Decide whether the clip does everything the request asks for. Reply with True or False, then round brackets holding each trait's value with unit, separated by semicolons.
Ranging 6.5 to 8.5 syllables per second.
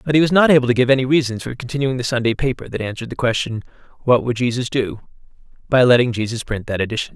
True (7.3 syllables/s)